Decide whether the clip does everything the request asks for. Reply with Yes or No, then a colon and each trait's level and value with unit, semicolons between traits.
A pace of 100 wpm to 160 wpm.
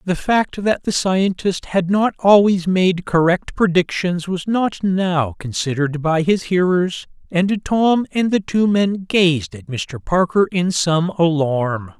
Yes: average, 155 wpm